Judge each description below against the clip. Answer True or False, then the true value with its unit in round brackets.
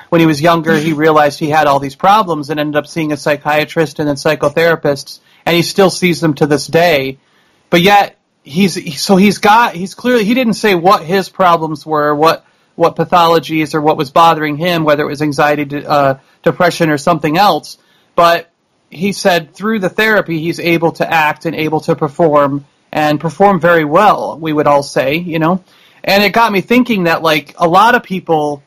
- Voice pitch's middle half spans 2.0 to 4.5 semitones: True (2.9 semitones)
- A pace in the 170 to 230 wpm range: True (200 wpm)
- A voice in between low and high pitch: True (165 Hz)